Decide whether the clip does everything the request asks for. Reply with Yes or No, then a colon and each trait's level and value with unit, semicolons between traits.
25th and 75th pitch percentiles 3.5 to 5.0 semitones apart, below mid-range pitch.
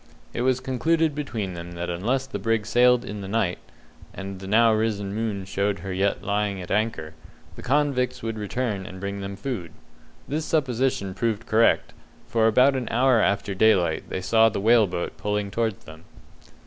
Yes: average, 3.9 semitones; low, 110 Hz